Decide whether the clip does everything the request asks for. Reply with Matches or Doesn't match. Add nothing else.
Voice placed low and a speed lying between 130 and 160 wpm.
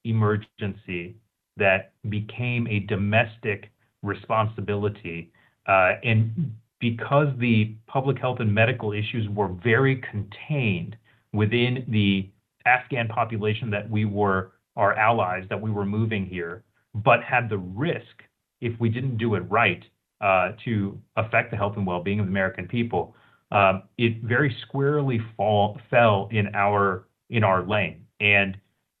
Matches